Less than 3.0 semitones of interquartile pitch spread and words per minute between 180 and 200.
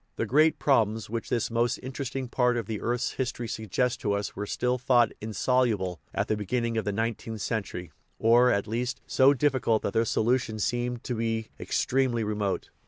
Yes: narrow, 2.5 semitones; average, 185 wpm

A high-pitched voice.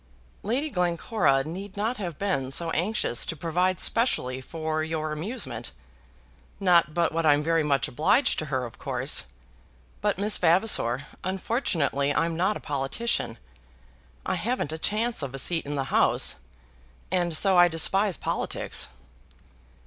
No: medium, 170 Hz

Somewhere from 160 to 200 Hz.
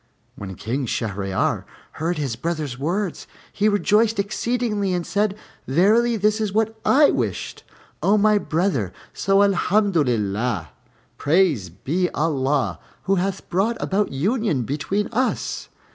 Yes: medium, 185 Hz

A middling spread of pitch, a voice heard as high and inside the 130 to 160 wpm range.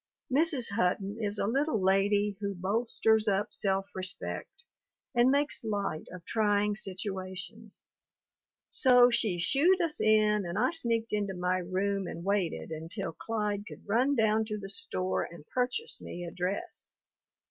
Yes: average, 3.3 semitones; high, 205 Hz; average, 145 wpm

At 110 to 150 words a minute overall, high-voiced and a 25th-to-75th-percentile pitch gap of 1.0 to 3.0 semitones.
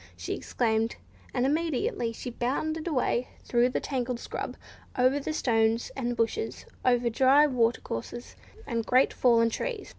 Yes: average, 140 wpm; high, 245 Hz; average, 2.7 semitones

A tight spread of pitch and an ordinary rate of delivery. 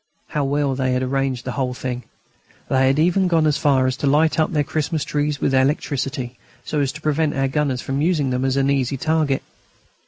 No: narrow, 2.3 semitones; fast, 215 wpm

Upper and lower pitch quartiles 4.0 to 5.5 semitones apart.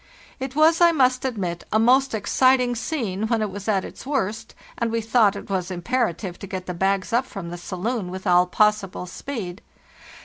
Yes: average, 5.1 semitones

